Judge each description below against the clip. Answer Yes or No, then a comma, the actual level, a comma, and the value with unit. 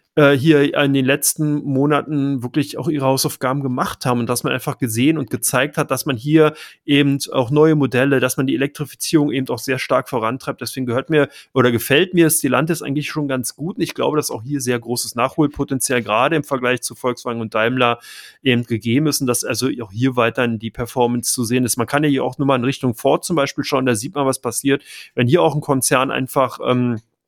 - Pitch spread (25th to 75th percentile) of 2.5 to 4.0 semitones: Yes, average, 2.8 semitones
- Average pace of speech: No, fast, 225 wpm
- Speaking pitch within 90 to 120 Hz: No, low, 135 Hz